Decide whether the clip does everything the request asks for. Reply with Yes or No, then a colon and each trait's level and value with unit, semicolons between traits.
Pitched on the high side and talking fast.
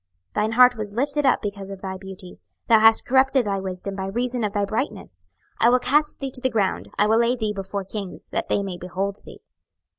Yes: high, 210 Hz; fast, 230 wpm